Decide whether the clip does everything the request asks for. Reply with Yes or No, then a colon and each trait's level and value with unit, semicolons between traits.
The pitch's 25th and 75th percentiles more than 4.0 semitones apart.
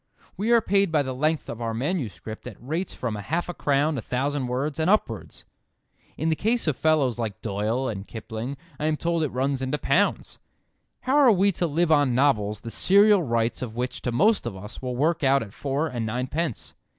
Yes: wide, 5.6 semitones